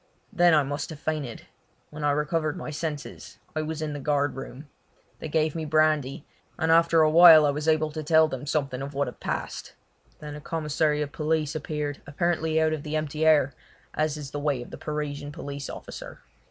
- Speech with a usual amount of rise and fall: No, narrow, 1.5 semitones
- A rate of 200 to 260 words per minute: Yes, fast, 205 wpm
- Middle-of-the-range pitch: Yes, medium, 150 Hz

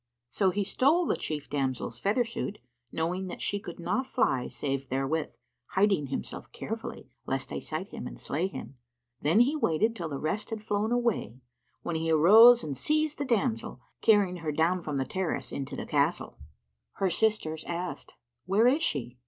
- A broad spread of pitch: Yes, wide, 6.6 semitones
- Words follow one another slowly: No, average, 175 wpm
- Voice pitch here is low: No, medium, 185 Hz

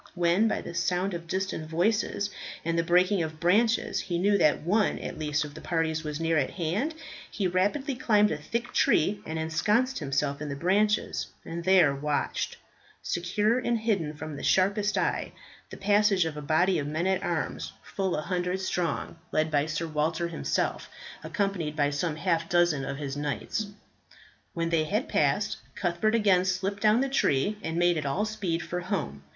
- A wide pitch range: No, average, 4.4 semitones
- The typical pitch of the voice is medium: Yes, medium, 175 Hz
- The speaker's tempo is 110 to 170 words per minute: No, average, 185 wpm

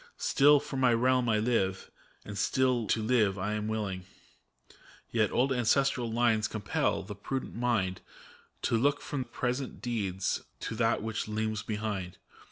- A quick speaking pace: No, average, 145 wpm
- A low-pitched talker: Yes, low, 110 Hz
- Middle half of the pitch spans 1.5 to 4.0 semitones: Yes, average, 3.1 semitones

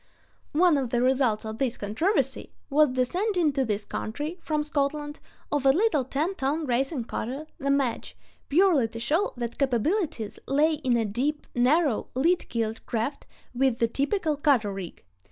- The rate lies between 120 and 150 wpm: No, average, 165 wpm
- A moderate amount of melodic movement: Yes, average, 4.3 semitones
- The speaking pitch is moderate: No, very high, 275 Hz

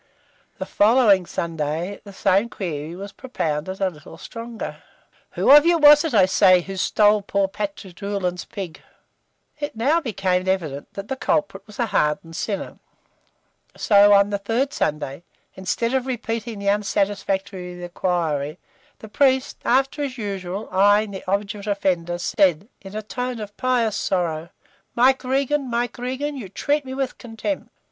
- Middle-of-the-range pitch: No, high, 200 Hz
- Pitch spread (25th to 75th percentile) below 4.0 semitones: No, average, 4.8 semitones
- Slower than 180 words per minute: Yes, average, 155 wpm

